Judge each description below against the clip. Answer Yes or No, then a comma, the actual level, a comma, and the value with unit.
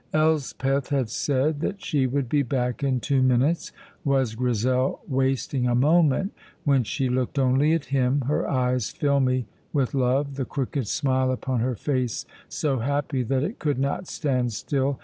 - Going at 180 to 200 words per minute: No, average, 165 wpm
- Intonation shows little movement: Yes, narrow, 2.0 semitones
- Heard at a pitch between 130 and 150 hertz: Yes, low, 135 Hz